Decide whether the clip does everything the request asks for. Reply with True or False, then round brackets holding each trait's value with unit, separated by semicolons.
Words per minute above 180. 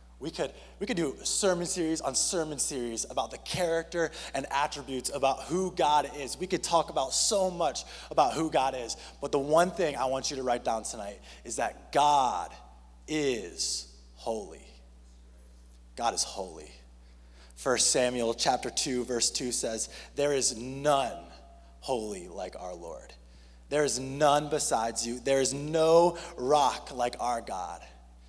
False (160 wpm)